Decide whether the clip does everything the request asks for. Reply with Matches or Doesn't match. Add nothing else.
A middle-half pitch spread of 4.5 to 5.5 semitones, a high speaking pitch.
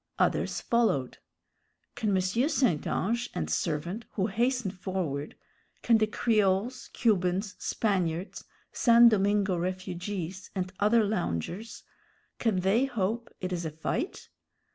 Doesn't match